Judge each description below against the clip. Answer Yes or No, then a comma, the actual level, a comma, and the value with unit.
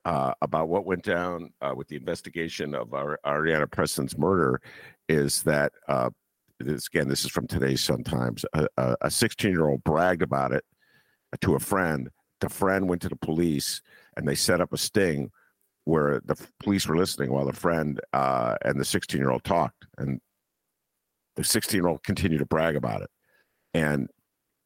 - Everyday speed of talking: Yes, average, 180 wpm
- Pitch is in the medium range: No, very low, 80 Hz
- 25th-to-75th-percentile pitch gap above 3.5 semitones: Yes, average, 4.1 semitones